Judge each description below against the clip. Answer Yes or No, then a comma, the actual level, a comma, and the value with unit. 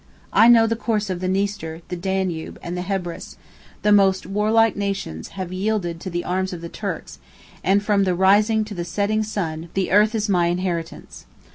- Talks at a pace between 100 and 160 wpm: No, average, 190 wpm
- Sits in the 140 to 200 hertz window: Yes, high, 190 Hz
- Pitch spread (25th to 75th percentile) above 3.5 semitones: No, average, 3.0 semitones